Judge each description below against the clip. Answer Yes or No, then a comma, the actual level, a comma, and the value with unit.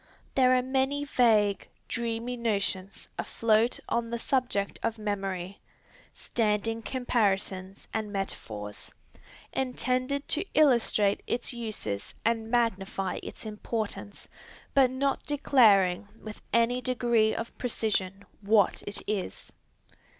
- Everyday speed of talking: No, slow, 105 wpm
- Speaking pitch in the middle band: No, high, 225 Hz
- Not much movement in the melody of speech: No, average, 3.7 semitones